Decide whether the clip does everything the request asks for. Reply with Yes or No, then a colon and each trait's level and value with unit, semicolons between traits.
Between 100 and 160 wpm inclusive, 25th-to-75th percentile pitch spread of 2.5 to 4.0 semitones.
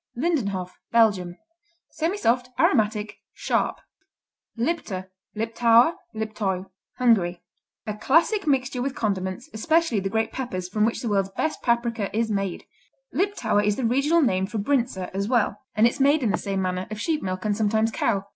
No: average, 155 wpm; average, 4.5 semitones